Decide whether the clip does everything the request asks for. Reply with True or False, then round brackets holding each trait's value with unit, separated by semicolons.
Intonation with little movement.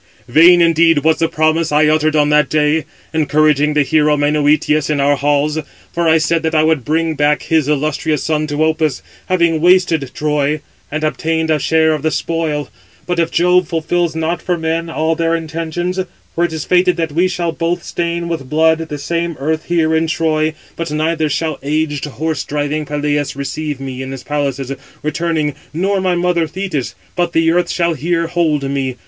True (2.0 semitones)